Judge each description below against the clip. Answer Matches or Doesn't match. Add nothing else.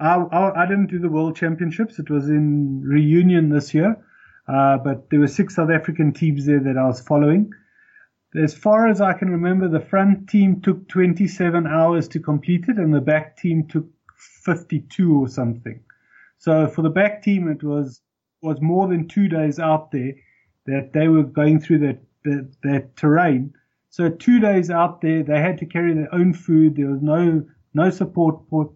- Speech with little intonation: Doesn't match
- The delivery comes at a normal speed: Matches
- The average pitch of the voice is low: Doesn't match